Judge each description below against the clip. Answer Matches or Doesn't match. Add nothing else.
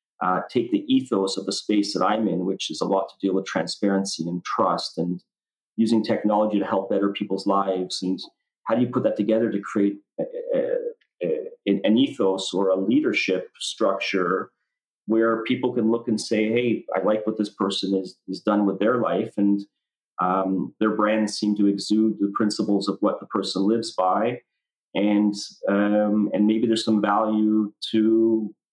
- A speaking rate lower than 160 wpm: Doesn't match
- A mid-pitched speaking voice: Doesn't match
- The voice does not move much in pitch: Matches